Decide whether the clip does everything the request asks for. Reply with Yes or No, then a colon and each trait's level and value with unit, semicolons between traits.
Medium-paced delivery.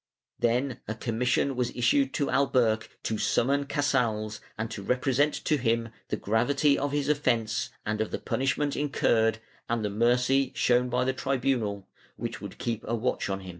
Yes: average, 170 wpm